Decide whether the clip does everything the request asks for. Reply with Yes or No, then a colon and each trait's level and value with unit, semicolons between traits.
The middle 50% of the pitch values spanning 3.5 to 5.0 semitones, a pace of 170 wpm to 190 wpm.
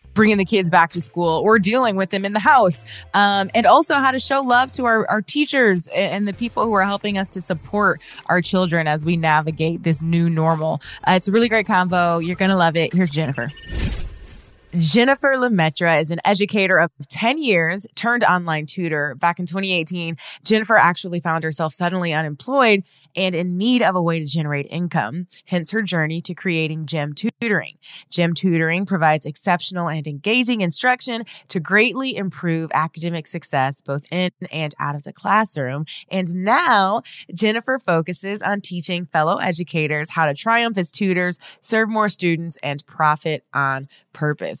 Yes: average, 4.3 semitones; average, 175 wpm